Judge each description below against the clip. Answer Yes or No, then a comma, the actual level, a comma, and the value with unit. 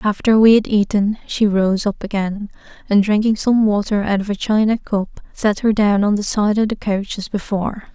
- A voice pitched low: No, high, 205 Hz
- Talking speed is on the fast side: Yes, fast, 210 wpm